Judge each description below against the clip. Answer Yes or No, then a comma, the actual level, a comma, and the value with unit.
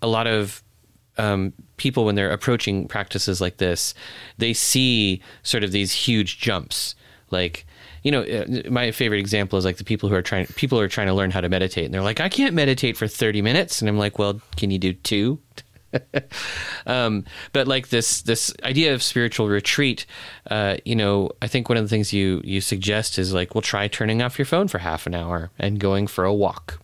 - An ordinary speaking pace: No, fast, 210 wpm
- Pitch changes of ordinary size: Yes, average, 3.3 semitones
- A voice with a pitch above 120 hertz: No, low, 105 Hz